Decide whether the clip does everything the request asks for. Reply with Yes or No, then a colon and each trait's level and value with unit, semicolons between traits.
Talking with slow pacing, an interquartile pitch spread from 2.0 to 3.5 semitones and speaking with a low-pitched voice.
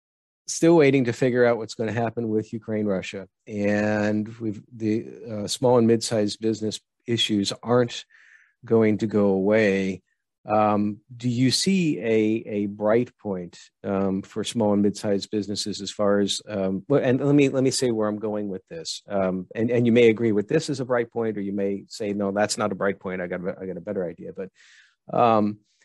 No: average, 200 wpm; narrow, 2.6 semitones; low, 110 Hz